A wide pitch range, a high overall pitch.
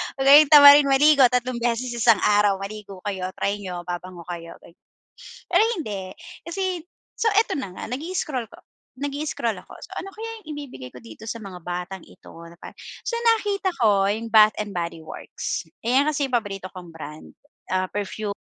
Yes: wide, 7.4 semitones; high, 215 Hz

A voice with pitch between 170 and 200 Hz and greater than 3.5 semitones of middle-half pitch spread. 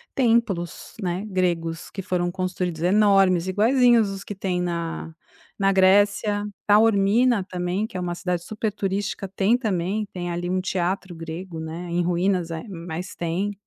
No: medium, 185 Hz; average, 2.7 semitones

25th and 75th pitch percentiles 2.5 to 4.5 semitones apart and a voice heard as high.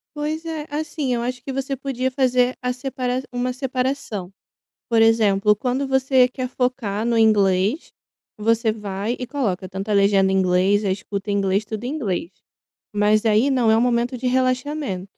Yes: average, 4.1 semitones; high, 235 Hz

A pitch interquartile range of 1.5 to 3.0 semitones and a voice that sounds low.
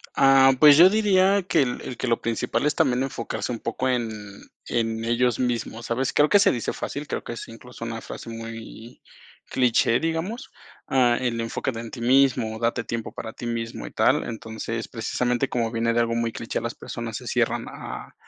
Yes: average, 2.7 semitones; low, 120 Hz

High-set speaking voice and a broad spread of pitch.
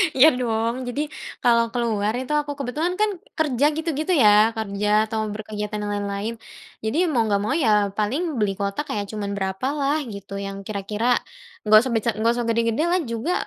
No: high, 225 Hz; average, 3.8 semitones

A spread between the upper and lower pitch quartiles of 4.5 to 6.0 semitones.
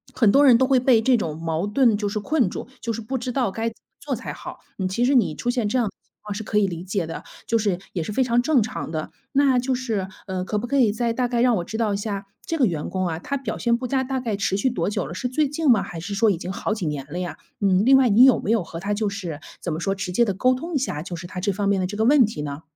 Yes: average, 5.0 semitones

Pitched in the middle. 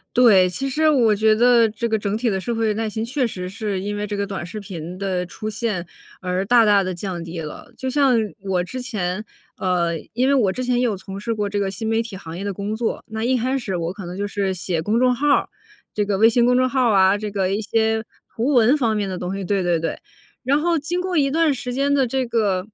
No: high, 215 Hz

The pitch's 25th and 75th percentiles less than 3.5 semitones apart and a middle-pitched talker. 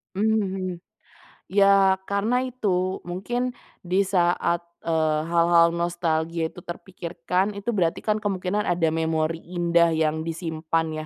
Yes: average, 2.9 semitones; medium, 175 Hz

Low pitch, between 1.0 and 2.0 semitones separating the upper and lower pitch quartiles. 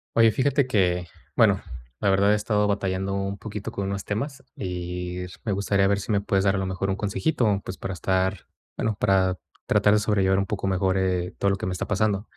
Yes: low, 100 Hz; narrow, 1.7 semitones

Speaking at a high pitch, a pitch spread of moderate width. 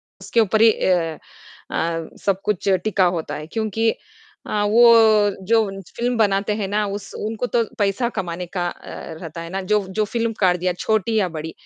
Yes: high, 205 Hz; average, 3.4 semitones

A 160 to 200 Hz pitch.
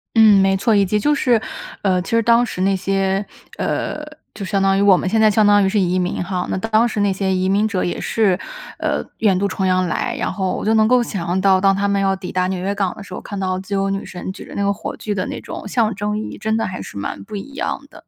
Yes: high, 195 Hz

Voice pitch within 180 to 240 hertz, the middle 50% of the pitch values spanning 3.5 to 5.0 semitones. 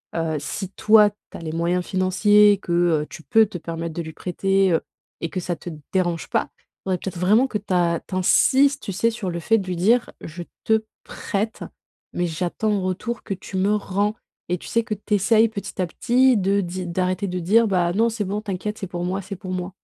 No: high, 190 Hz; average, 3.1 semitones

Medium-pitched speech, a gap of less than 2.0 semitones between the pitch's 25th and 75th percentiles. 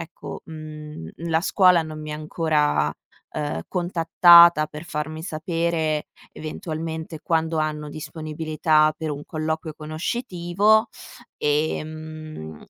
Yes: medium, 155 Hz; narrow, 1.4 semitones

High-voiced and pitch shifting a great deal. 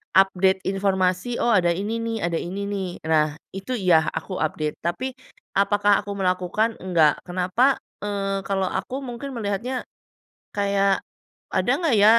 No: high, 195 Hz; average, 3.0 semitones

